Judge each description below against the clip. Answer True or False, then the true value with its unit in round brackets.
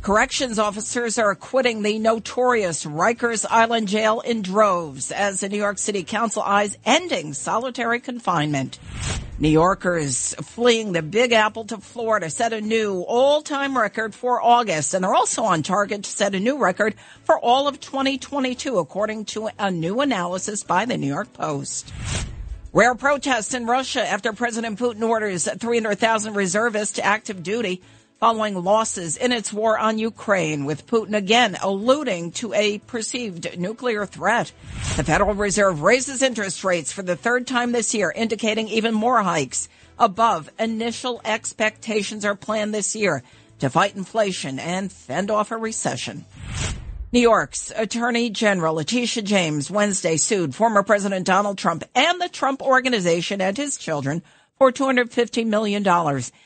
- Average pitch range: True (3.7 semitones)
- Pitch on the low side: False (215 Hz)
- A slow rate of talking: False (150 wpm)